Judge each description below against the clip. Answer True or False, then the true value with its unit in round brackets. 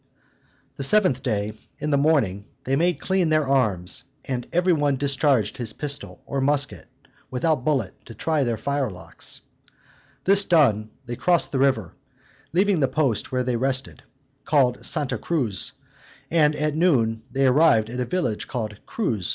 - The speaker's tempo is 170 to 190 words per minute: False (160 wpm)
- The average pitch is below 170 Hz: True (135 Hz)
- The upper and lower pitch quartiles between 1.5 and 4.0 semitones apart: False (4.6 semitones)